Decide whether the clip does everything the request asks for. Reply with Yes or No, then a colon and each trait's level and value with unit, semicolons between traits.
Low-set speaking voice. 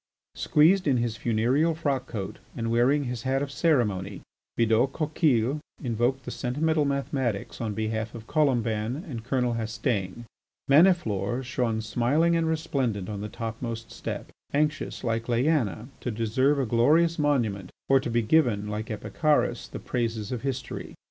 Yes: low, 120 Hz